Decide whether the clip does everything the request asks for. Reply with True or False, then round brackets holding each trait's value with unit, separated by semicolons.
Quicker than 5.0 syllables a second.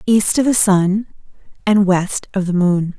False (3.9 syllables/s)